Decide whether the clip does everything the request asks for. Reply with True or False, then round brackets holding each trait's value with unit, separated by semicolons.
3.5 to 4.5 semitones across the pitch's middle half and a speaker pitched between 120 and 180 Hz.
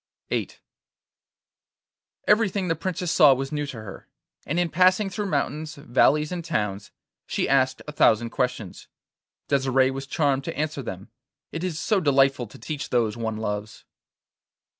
False (5.3 semitones; 140 Hz)